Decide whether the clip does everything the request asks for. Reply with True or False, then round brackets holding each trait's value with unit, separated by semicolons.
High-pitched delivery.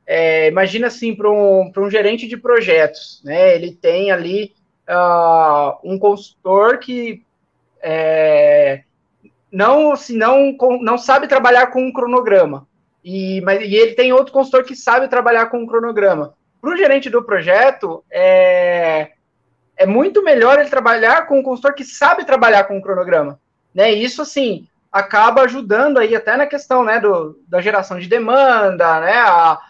True (215 Hz)